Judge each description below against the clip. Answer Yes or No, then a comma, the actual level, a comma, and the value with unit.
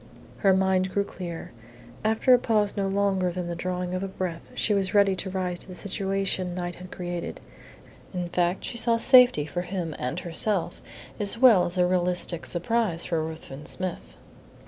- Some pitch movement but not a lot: No, narrow, 2.3 semitones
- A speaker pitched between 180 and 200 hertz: Yes, medium, 185 Hz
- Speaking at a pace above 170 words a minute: Yes, average, 180 wpm